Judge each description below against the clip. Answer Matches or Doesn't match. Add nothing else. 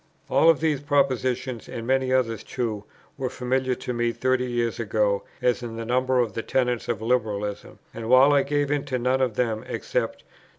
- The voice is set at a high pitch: Doesn't match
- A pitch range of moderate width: Doesn't match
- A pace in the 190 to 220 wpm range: Matches